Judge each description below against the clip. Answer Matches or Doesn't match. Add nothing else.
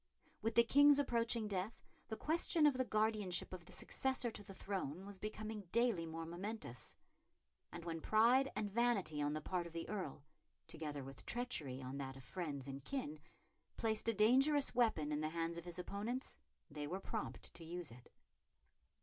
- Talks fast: Doesn't match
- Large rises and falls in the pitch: Matches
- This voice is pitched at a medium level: Doesn't match